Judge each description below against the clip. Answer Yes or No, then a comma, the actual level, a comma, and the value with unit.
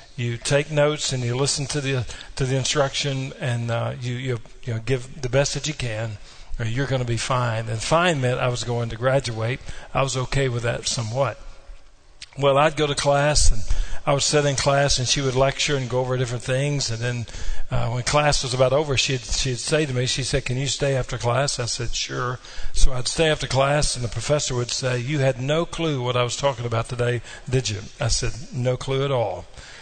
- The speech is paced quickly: Yes, fast, 230 wpm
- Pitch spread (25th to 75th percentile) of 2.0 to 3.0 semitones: Yes, average, 2.7 semitones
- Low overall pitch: Yes, low, 130 Hz